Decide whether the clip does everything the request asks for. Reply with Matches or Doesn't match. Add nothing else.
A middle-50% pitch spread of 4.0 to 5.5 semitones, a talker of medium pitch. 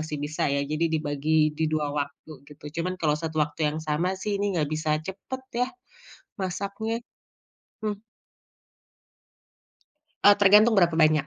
Matches